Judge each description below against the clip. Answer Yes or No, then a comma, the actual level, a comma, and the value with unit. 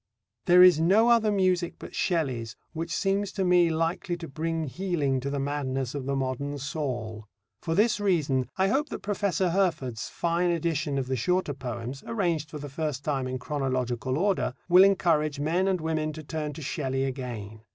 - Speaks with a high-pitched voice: No, medium, 155 Hz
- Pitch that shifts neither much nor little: Yes, average, 5.0 semitones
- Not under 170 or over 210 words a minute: Yes, average, 185 wpm